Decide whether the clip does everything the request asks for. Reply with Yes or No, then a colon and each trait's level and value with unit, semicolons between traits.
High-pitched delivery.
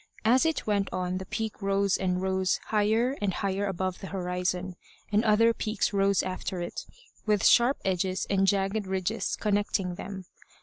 Yes: high, 195 Hz